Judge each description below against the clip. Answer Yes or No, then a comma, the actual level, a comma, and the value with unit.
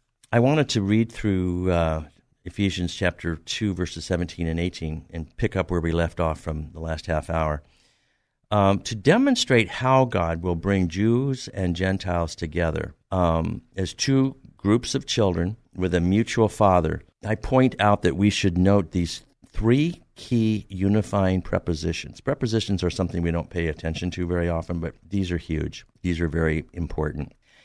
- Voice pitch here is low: Yes, very low, 90 Hz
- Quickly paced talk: No, average, 165 wpm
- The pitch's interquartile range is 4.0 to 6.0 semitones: Yes, average, 4.4 semitones